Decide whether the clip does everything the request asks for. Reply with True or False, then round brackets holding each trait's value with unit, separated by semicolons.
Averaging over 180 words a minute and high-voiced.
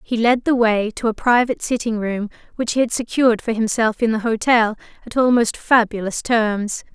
True (190 wpm; 225 Hz)